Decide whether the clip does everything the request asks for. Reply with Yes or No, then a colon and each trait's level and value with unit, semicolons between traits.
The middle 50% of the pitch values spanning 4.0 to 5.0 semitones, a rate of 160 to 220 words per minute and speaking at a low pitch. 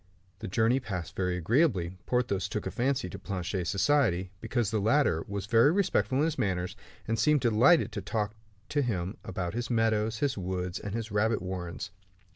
Yes: average, 4.7 semitones; average, 180 wpm; low, 105 Hz